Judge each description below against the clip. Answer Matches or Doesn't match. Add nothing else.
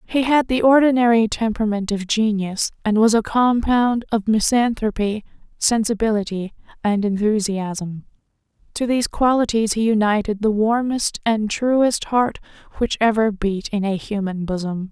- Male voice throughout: Doesn't match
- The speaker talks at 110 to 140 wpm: Matches